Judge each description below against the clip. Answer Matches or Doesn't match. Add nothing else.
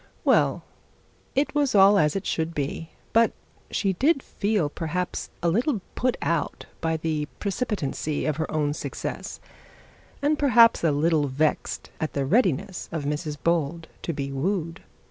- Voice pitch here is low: Doesn't match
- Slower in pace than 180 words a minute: Matches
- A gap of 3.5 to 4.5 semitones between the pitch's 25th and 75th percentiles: Doesn't match